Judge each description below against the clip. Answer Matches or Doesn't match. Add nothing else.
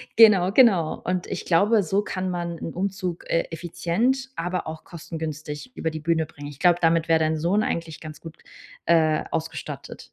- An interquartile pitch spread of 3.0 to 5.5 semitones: Doesn't match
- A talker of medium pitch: Matches